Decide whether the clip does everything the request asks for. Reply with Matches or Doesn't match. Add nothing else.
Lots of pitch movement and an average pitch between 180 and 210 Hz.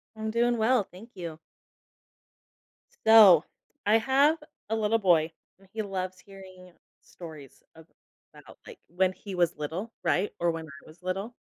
Doesn't match